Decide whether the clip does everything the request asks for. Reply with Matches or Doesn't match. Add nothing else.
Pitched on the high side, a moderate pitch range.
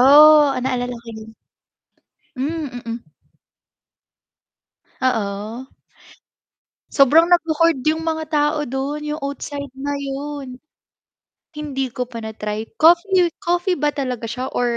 Matches